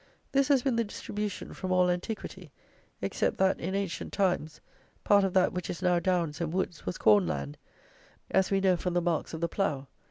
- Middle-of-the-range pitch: Yes, medium, 180 Hz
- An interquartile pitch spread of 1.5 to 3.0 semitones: Yes, average, 2.7 semitones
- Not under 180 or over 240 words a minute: Yes, average, 200 wpm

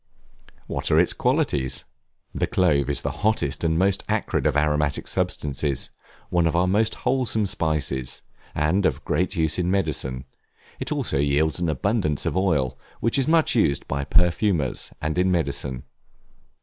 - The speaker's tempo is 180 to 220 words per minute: No, average, 155 wpm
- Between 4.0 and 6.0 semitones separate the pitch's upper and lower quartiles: Yes, average, 4.8 semitones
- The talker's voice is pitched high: No, very low, 80 Hz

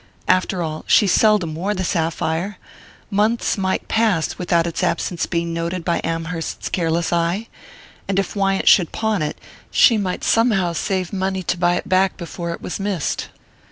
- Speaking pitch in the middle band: Yes, medium, 180 Hz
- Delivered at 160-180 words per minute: Yes, average, 165 wpm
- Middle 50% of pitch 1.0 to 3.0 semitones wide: Yes, average, 2.7 semitones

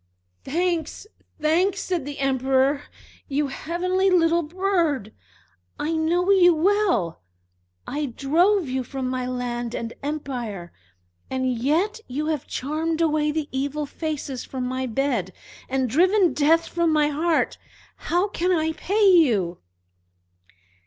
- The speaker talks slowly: Yes, slow, 125 wpm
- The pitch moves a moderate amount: Yes, average, 4.7 semitones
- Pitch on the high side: Yes, very high, 300 Hz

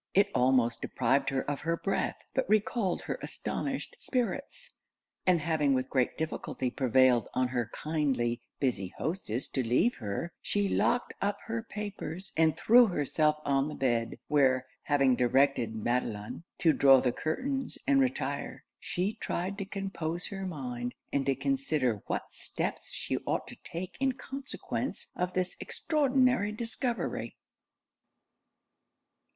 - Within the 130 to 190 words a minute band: Yes, average, 140 wpm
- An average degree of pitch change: No, wide, 7.9 semitones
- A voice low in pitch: No, medium, 155 Hz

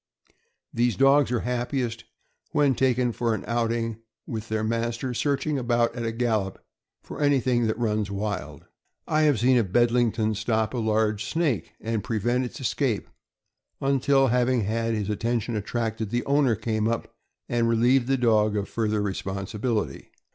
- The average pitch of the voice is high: No, low, 115 Hz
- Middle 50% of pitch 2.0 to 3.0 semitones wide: Yes, narrow, 2.4 semitones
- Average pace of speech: Yes, average, 155 wpm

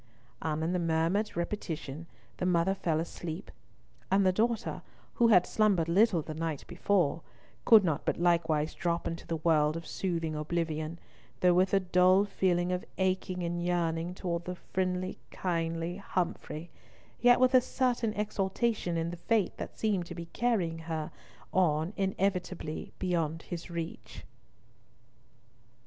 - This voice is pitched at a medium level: Yes, medium, 175 Hz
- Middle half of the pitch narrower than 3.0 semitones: Yes, narrow, 2.5 semitones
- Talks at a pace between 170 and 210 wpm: No, average, 145 wpm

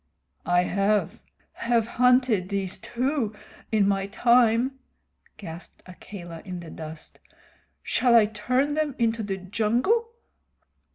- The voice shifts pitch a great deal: No, average, 4.5 semitones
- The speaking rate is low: Yes, slow, 115 wpm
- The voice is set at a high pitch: Yes, high, 215 Hz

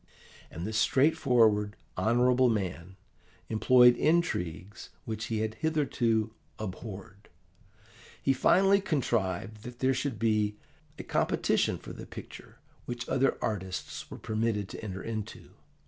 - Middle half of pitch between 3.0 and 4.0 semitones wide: Yes, average, 3.5 semitones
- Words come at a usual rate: No, slow, 120 wpm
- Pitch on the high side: No, low, 110 Hz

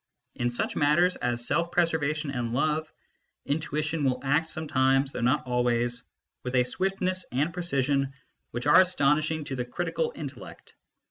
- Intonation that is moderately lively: Yes, average, 4.3 semitones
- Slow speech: No, average, 145 wpm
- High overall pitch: No, medium, 145 Hz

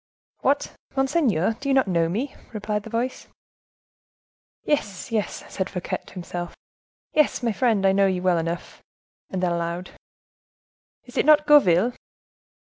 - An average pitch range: No, wide, 6.3 semitones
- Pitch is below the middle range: No, high, 205 Hz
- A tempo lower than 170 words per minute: Yes, average, 145 wpm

